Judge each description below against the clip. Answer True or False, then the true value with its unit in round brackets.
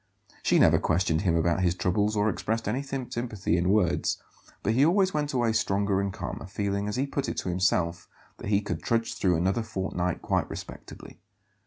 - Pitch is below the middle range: True (100 Hz)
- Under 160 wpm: False (190 wpm)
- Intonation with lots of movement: False (4.2 semitones)